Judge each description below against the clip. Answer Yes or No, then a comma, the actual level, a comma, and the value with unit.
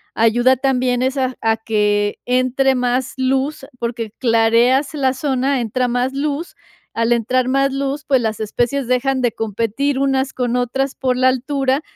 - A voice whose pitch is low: No, very high, 255 Hz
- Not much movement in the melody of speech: Yes, narrow, 2.2 semitones